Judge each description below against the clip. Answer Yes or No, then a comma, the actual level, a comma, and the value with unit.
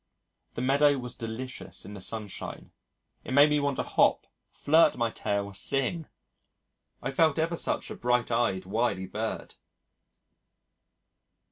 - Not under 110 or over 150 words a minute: Yes, slow, 135 wpm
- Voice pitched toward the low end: Yes, low, 125 Hz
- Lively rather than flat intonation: No, average, 4.3 semitones